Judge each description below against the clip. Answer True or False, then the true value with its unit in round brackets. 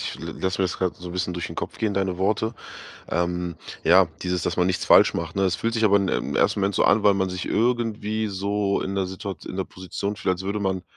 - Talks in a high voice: False (95 Hz)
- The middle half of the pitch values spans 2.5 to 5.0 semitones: False (2.0 semitones)